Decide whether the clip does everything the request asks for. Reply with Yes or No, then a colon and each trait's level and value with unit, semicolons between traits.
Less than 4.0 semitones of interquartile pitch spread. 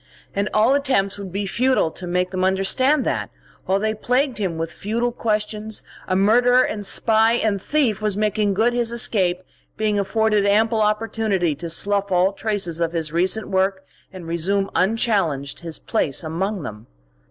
Yes: average, 3.1 semitones